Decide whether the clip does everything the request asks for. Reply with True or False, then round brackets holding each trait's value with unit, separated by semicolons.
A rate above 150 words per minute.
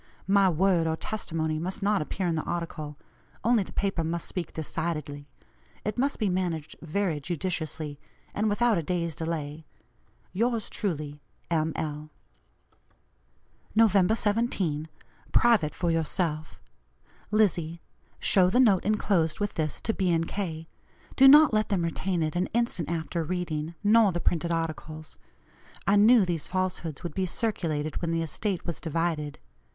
False (145 wpm)